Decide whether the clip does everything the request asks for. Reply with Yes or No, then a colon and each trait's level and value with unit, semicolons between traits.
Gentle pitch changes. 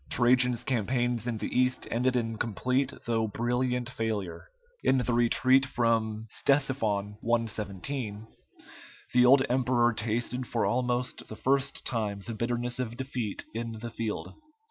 Yes: narrow, 2.3 semitones